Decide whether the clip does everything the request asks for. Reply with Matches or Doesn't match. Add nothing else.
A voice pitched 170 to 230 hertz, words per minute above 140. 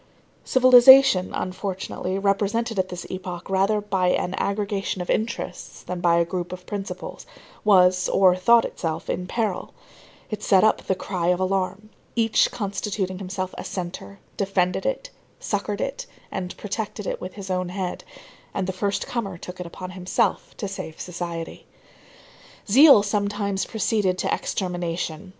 Matches